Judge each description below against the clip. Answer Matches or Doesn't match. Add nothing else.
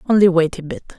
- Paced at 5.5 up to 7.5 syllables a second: Matches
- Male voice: Doesn't match